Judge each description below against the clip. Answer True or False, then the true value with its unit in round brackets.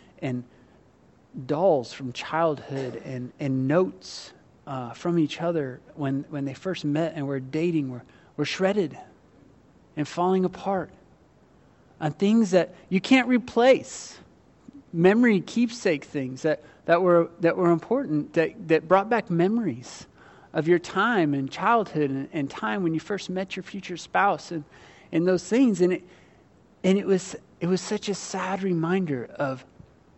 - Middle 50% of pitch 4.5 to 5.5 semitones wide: True (5.0 semitones)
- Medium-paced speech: True (150 wpm)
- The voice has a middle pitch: True (170 Hz)